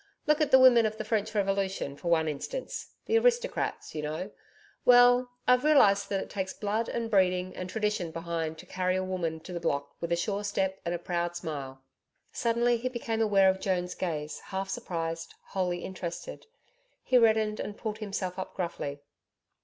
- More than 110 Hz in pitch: Yes, high, 190 Hz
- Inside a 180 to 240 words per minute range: Yes, average, 185 wpm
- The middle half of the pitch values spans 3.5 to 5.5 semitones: Yes, average, 4.4 semitones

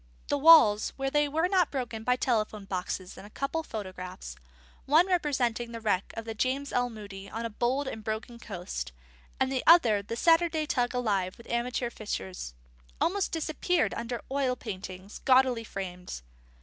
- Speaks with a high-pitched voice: Yes, high, 235 Hz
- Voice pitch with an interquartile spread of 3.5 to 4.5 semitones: No, average, 5.2 semitones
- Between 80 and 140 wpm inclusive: No, average, 165 wpm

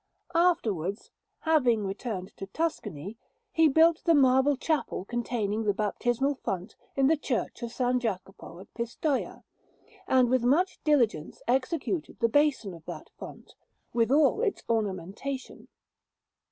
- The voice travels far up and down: Yes, wide, 5.9 semitones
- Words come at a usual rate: No, slow, 130 wpm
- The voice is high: Yes, high, 245 Hz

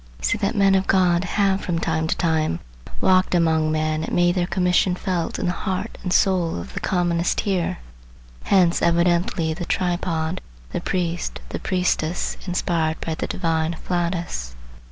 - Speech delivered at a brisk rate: No, average, 165 wpm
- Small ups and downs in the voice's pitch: Yes, narrow, 2.2 semitones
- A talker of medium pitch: Yes, medium, 175 Hz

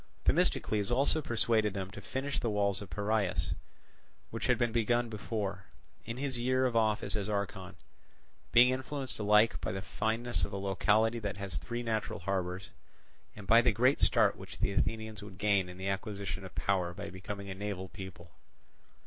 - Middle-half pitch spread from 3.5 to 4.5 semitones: No, average, 3.0 semitones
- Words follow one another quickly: No, average, 175 wpm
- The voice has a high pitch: No, low, 105 Hz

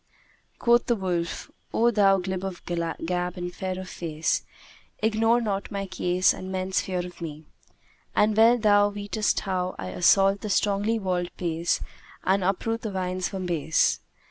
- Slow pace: No, average, 160 wpm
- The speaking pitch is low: No, high, 190 Hz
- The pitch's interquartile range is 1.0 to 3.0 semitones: Yes, narrow, 2.5 semitones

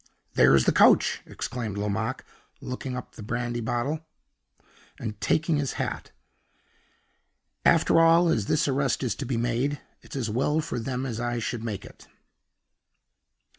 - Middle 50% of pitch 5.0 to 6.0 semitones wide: No, average, 3.6 semitones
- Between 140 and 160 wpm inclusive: Yes, average, 145 wpm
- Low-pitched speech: Yes, low, 120 Hz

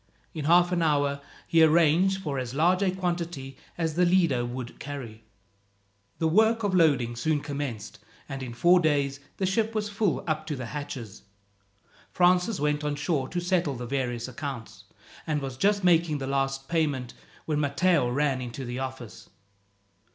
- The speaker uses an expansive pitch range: No, average, 4.8 semitones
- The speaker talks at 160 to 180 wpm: Yes, average, 165 wpm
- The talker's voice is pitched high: No, medium, 150 Hz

